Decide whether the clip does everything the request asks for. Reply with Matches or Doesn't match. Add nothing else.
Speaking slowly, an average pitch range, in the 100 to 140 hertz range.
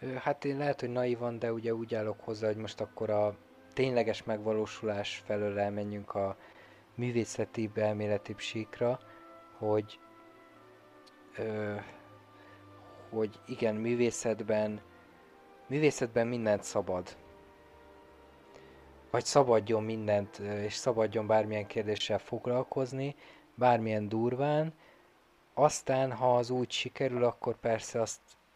Matches